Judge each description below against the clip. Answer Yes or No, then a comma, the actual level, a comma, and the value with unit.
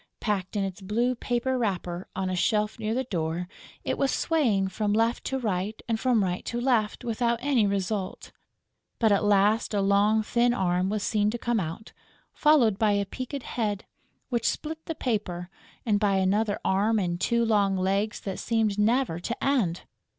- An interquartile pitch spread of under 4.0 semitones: Yes, average, 3.4 semitones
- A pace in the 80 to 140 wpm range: No, average, 180 wpm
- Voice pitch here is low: No, high, 210 Hz